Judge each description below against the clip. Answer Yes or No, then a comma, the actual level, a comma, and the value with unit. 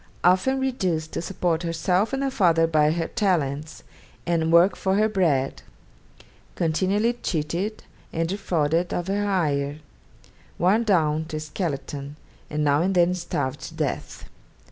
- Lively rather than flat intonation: No, average, 3.9 semitones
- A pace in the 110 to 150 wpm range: Yes, average, 145 wpm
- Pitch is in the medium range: Yes, medium, 170 Hz